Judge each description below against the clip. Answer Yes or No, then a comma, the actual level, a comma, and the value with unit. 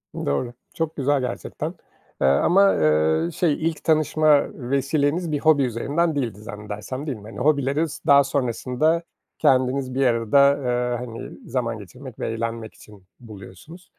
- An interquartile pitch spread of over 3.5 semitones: Yes, average, 4.3 semitones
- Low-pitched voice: Yes, low, 130 Hz